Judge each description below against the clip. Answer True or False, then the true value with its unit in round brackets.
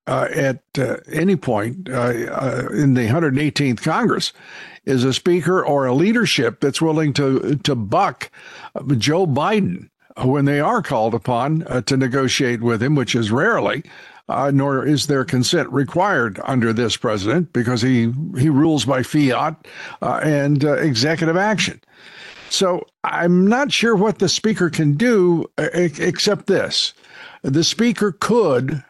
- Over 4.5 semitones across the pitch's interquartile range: True (4.9 semitones)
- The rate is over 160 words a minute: False (145 wpm)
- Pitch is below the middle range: False (145 Hz)